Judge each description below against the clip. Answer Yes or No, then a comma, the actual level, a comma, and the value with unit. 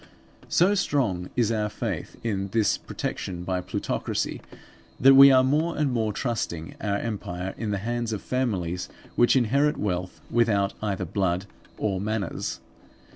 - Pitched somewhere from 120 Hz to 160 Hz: No, low, 105 Hz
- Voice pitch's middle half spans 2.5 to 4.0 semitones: No, average, 4.5 semitones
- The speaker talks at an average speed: Yes, average, 145 wpm